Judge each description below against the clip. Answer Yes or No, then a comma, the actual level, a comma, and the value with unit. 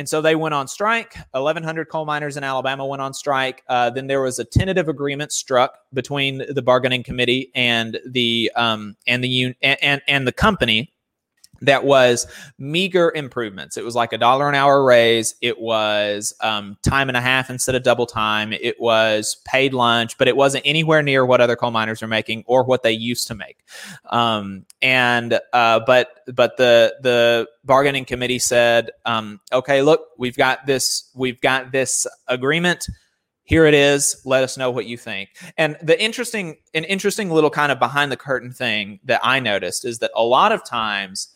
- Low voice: Yes, low, 130 Hz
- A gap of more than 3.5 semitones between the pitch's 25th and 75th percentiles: No, average, 3.2 semitones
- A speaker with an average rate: Yes, average, 190 wpm